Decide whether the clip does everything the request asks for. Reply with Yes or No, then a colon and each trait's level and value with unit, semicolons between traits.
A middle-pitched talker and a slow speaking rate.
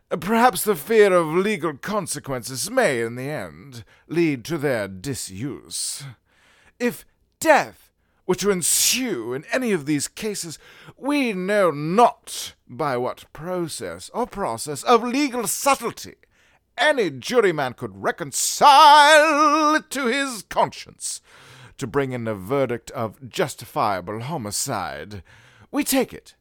Yes: medium, 180 Hz; slow, 125 wpm